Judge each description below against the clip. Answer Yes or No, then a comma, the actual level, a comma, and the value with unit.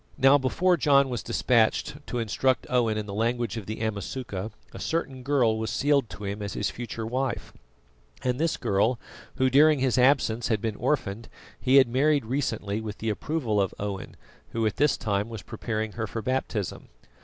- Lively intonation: No, average, 3.7 semitones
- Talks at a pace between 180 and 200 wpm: Yes, average, 185 wpm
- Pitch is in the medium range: No, low, 115 Hz